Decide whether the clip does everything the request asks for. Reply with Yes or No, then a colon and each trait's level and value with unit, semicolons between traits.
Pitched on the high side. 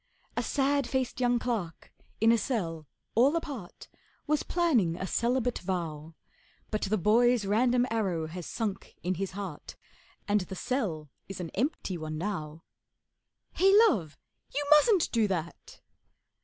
Yes: high, 210 Hz